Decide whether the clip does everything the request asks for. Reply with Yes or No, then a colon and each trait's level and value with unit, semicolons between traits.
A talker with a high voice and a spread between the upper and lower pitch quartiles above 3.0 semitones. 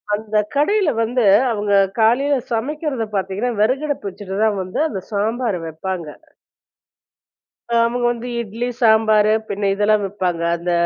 Yes: high, 220 Hz; average, 3.5 semitones